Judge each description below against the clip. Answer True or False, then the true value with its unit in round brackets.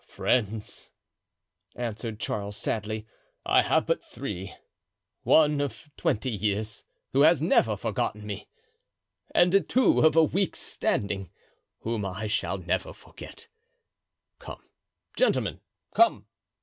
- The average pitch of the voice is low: True (110 Hz)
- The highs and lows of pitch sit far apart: True (6.6 semitones)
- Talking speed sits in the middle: False (110 wpm)